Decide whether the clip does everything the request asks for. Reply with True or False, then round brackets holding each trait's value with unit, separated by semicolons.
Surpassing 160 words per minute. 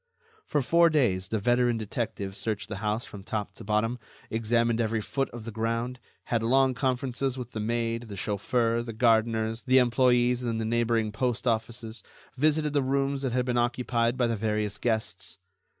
True (180 wpm)